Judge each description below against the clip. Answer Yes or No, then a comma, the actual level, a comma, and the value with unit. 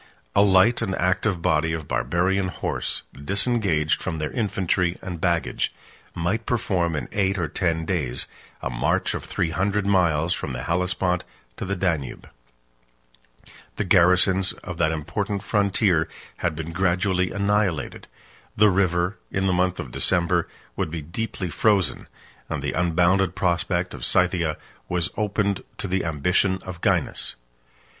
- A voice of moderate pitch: No, very low, 90 Hz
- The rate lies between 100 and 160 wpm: Yes, average, 145 wpm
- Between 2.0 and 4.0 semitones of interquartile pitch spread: Yes, average, 2.7 semitones